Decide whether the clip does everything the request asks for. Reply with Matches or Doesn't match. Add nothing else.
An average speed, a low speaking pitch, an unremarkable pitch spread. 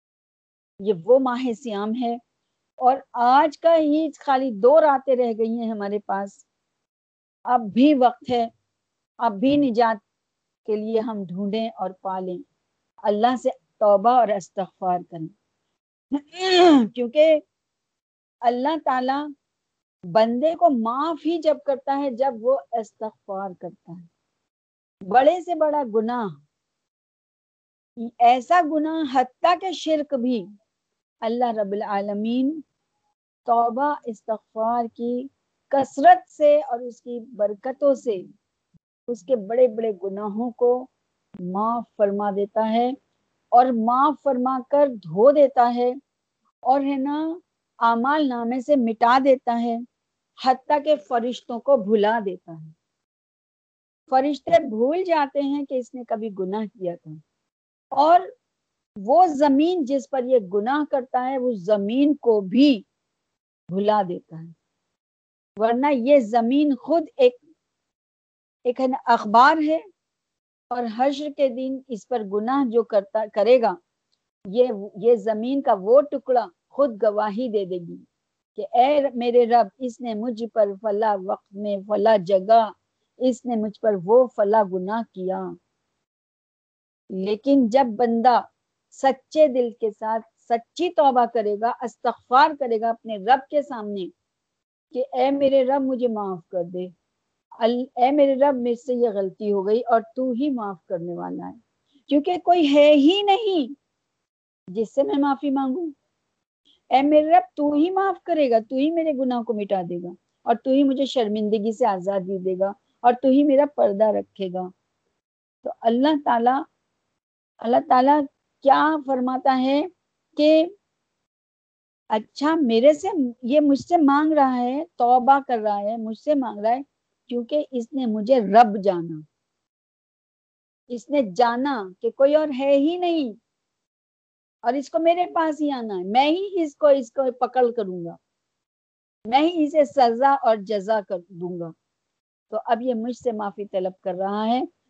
Doesn't match